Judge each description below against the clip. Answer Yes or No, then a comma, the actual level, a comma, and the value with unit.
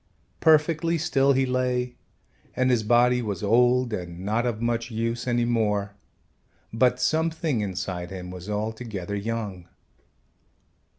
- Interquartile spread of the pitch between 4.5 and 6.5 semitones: No, average, 3.6 semitones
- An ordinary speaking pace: No, slow, 125 wpm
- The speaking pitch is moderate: No, low, 115 Hz